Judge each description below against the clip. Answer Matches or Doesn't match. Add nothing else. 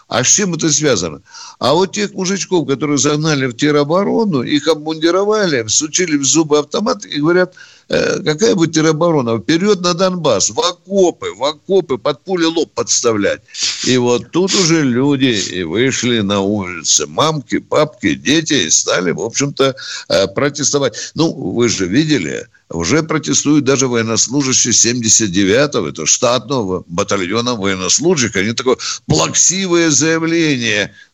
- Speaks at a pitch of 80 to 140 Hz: Doesn't match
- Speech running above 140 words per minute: Doesn't match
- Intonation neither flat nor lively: Doesn't match